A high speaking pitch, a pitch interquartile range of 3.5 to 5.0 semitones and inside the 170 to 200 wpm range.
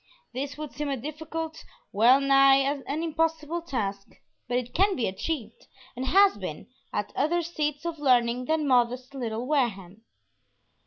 No: very high, 275 Hz; average, 4.4 semitones; average, 150 wpm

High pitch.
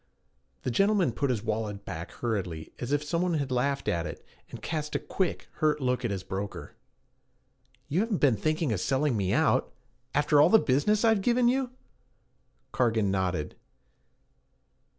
No: low, 135 Hz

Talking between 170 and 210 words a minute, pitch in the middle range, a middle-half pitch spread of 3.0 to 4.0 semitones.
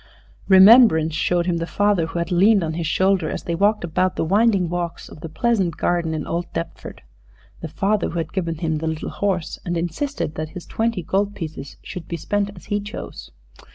Yes: fast, 205 wpm; medium, 175 Hz; average, 3.6 semitones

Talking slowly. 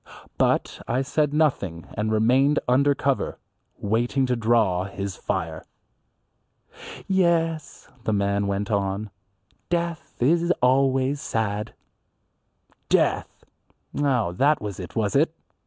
Yes: slow, 110 wpm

